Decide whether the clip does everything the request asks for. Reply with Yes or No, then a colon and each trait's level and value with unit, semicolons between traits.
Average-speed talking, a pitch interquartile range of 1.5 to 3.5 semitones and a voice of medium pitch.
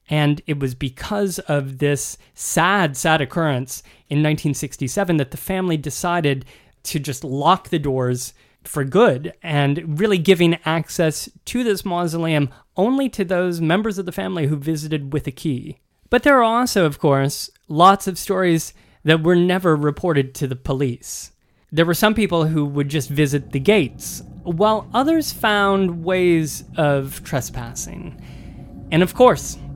No: average, 155 wpm; average, 4.6 semitones; medium, 160 Hz